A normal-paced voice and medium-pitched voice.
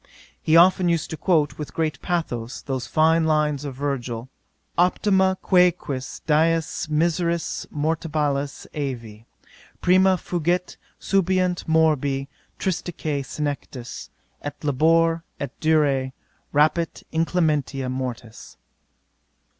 No: slow, 100 wpm; medium, 155 Hz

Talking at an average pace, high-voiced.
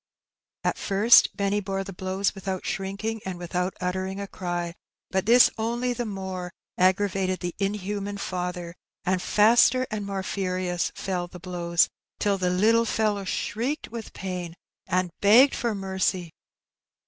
Yes: average, 145 wpm; high, 195 Hz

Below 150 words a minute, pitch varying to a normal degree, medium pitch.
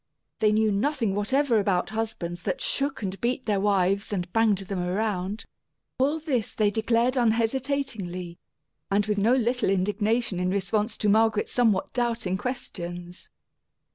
No: average, 140 wpm; average, 3.6 semitones; high, 215 Hz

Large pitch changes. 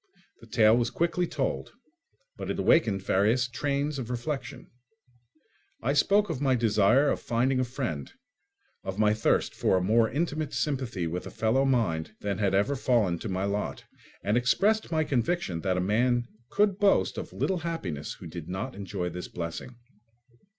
Yes: wide, 6.3 semitones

